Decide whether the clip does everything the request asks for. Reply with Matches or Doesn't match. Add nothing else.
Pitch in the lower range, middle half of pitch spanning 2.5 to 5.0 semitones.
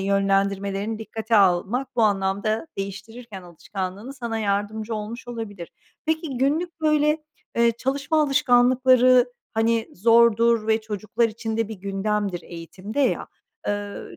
Doesn't match